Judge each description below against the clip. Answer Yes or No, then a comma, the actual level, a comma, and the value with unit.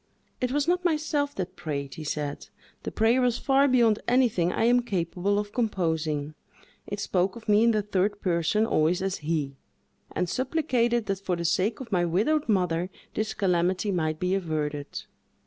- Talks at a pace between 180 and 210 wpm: No, average, 170 wpm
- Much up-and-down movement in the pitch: Yes, wide, 5.7 semitones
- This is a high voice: Yes, high, 195 Hz